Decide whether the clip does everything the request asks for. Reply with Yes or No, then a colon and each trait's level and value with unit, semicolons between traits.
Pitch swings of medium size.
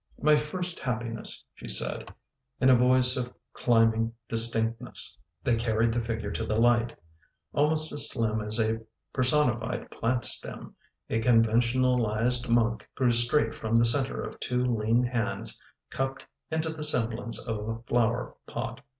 No: narrow, 2.0 semitones